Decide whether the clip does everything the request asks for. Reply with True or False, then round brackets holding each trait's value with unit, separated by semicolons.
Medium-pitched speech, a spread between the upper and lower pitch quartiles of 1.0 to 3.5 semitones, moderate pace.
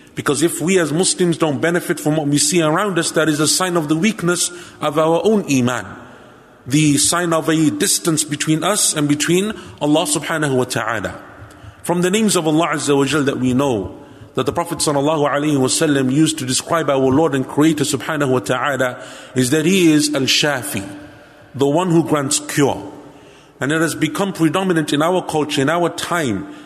True (155 Hz; 3.0 semitones; 195 wpm)